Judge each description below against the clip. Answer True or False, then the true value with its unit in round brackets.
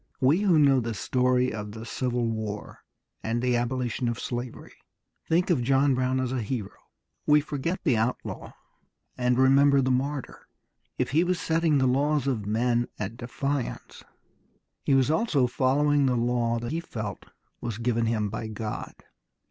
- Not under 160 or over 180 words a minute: True (165 wpm)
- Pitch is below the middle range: True (125 Hz)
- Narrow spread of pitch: False (3.2 semitones)